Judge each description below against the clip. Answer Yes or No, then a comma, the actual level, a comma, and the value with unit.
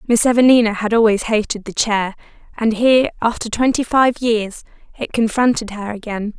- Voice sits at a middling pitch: No, high, 225 Hz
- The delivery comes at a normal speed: Yes, average, 160 wpm